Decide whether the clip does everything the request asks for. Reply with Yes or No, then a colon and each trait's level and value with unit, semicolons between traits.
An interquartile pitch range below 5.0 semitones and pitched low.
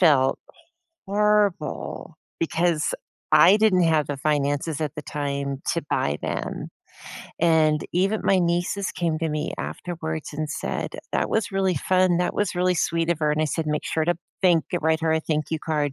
No: average, 2.8 semitones; medium, 160 Hz